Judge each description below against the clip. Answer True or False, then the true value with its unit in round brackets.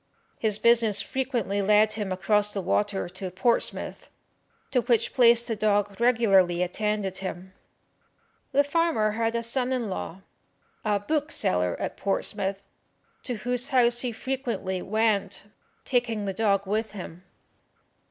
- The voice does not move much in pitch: False (3.4 semitones)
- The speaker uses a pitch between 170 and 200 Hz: False (215 Hz)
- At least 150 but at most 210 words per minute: False (135 wpm)